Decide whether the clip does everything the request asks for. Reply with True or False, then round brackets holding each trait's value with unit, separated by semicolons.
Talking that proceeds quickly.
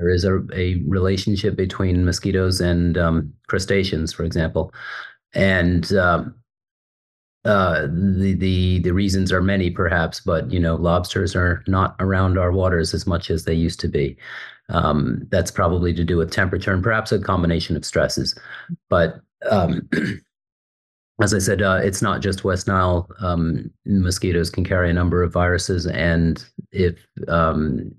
False (155 wpm)